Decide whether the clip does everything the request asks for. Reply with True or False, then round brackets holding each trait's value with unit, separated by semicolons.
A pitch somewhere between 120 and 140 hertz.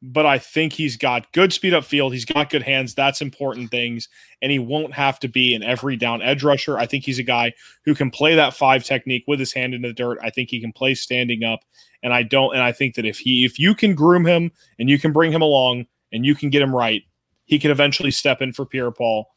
True (135 Hz)